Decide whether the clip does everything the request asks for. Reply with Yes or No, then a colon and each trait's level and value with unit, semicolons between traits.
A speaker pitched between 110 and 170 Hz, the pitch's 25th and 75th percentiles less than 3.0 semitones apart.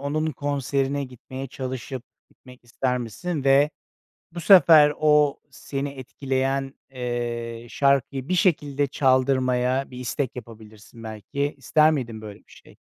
Yes: low, 135 Hz; narrow, 2.5 semitones